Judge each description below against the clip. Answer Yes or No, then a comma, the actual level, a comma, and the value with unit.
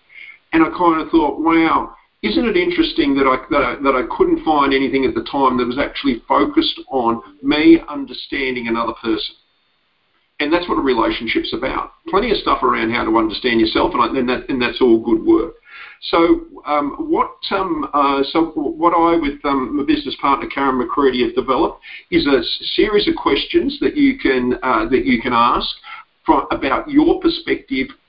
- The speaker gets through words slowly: No, average, 185 wpm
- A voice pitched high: Yes, very high, 320 Hz